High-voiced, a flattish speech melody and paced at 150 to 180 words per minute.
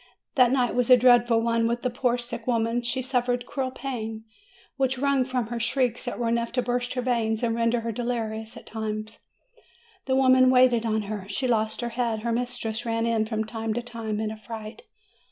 No: high, 235 Hz; narrow, 1.9 semitones; fast, 205 wpm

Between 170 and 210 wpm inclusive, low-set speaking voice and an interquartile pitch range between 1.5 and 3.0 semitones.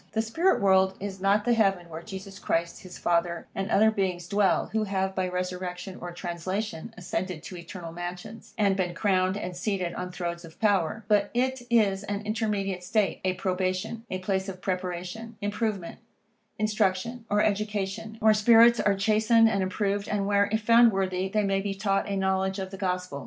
No: average, 185 wpm; high, 195 Hz; narrow, 2.5 semitones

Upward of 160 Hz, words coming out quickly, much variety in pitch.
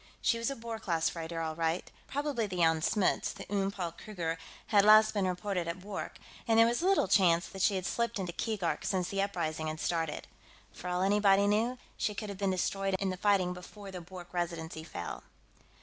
No: high, 190 Hz; fast, 210 wpm; average, 3.3 semitones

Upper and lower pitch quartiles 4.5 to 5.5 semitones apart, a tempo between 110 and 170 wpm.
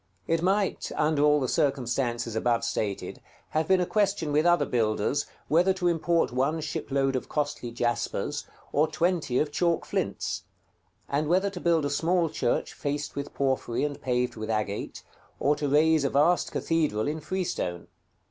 Yes: average, 4.9 semitones; average, 165 wpm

